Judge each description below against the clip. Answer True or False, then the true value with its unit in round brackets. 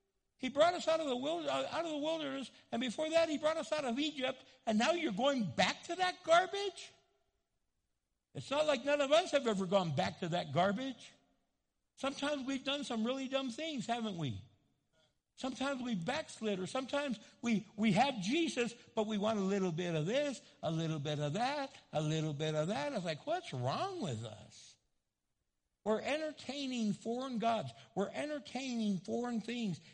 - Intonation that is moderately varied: False (7.0 semitones)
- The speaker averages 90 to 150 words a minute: False (180 wpm)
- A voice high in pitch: True (245 Hz)